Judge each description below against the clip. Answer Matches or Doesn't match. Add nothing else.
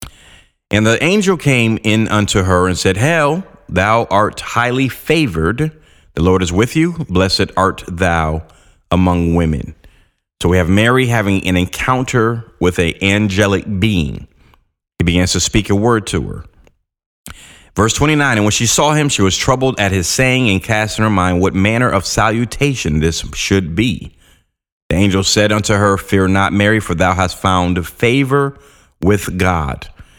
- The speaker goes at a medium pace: Matches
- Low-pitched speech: Matches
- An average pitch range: Matches